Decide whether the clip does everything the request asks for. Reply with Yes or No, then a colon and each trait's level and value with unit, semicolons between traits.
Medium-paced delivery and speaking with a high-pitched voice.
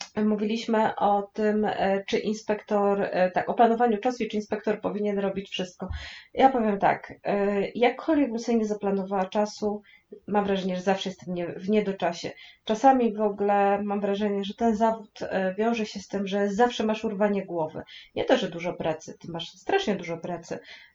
No: fast, 165 wpm; high, 205 Hz